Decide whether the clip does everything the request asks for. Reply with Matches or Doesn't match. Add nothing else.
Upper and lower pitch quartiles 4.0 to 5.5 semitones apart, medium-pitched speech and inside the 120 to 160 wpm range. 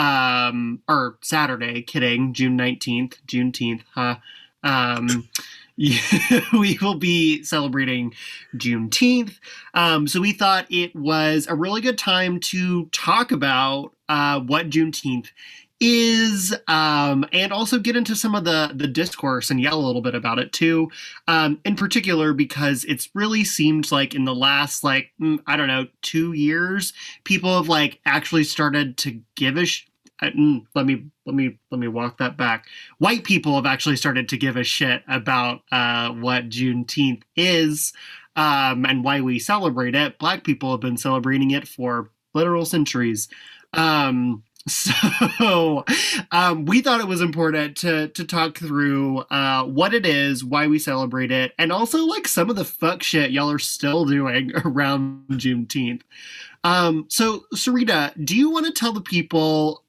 Matches